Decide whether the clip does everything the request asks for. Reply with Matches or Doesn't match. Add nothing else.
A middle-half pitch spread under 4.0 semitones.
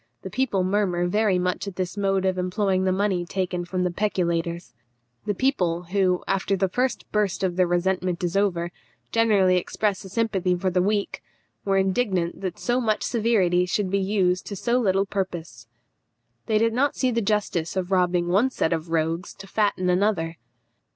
Matches